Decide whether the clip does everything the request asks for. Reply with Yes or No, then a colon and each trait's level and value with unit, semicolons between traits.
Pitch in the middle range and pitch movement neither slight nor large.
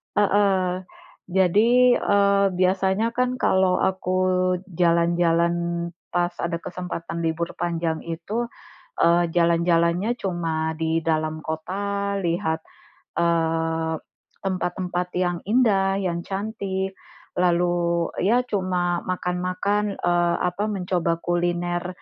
No: medium, 175 Hz; narrow, 2.1 semitones